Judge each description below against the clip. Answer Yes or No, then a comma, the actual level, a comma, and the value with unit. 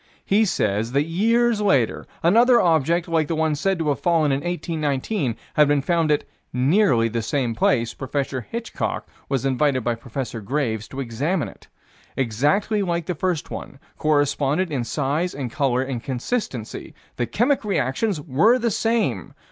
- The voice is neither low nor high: Yes, medium, 145 Hz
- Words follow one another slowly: No, average, 160 wpm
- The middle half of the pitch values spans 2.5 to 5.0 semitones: No, wide, 5.6 semitones